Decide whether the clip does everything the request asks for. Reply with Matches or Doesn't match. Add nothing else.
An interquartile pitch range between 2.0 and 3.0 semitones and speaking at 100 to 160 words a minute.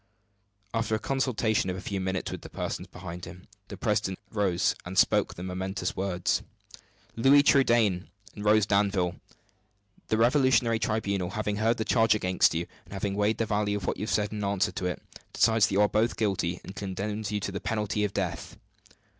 Doesn't match